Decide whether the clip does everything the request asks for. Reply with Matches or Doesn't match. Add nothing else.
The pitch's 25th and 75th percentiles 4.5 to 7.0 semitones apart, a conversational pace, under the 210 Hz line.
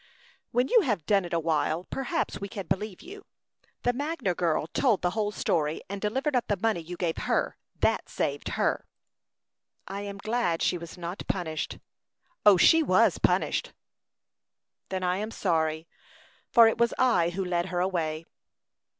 Matches